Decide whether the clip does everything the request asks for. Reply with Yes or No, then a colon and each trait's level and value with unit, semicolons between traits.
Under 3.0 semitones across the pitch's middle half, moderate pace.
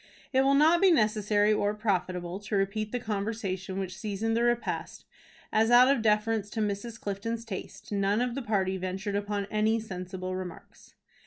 Yes: narrow, 2.6 semitones; average, 170 wpm